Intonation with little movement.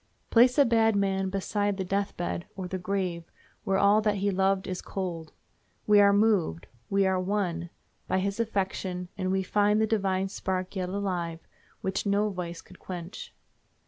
Yes: narrow, 1.9 semitones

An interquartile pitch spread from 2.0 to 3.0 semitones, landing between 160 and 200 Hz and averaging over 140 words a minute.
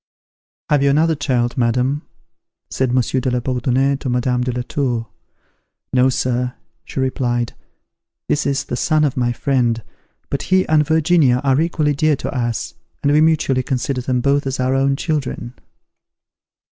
No: narrow, 2.5 semitones; low, 130 Hz; average, 160 wpm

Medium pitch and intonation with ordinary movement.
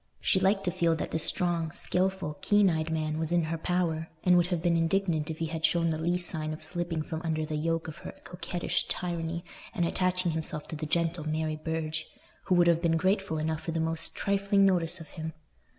No: medium, 165 Hz; narrow, 1.9 semitones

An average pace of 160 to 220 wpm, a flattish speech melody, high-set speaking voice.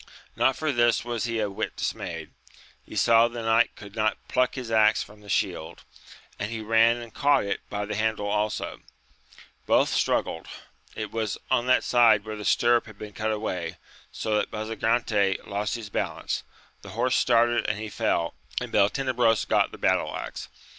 No: average, 180 wpm; narrow, 2.3 semitones; low, 110 Hz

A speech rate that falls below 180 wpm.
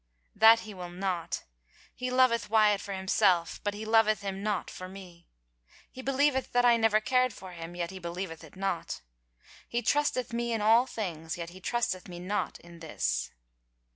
No: average, 185 wpm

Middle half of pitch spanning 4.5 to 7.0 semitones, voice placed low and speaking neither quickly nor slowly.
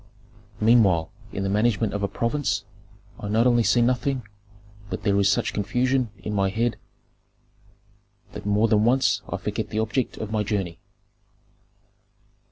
No: average, 2.9 semitones; low, 110 Hz; average, 150 wpm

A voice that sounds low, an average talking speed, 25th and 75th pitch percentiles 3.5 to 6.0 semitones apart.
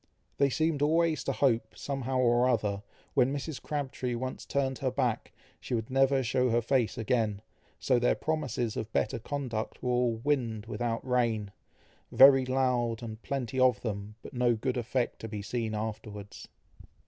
No: low, 125 Hz; average, 165 wpm; average, 3.0 semitones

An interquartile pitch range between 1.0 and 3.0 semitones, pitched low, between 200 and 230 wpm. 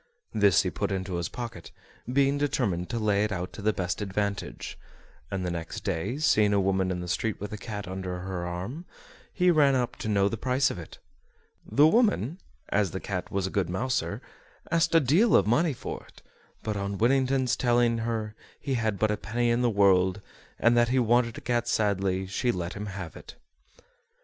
No: average, 4.5 semitones; low, 105 Hz; fast, 205 wpm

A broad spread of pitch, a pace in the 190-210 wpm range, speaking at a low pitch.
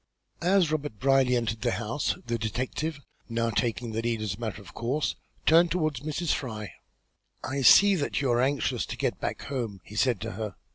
No: average, 4.6 semitones; average, 195 wpm; low, 125 Hz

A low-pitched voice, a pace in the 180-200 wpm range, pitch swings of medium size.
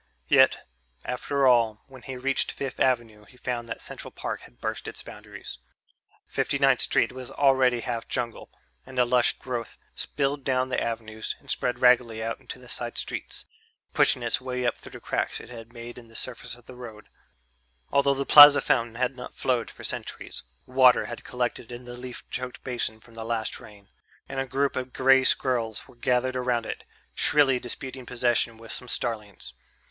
No: low, 125 Hz; average, 185 wpm; narrow, 1.8 semitones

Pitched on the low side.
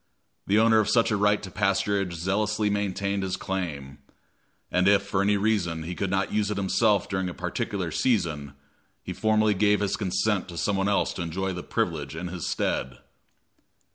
Yes: very low, 95 Hz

